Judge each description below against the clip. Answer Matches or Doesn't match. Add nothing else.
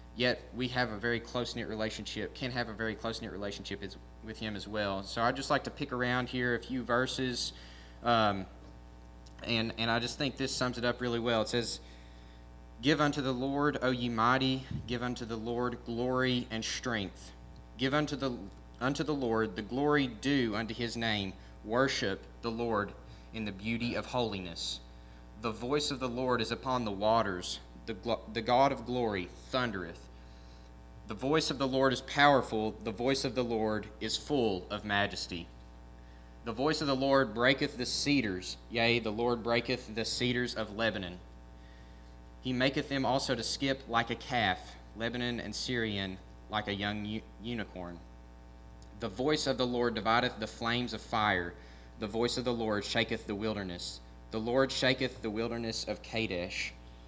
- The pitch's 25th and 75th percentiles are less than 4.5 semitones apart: Doesn't match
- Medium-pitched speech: Doesn't match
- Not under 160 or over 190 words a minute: Matches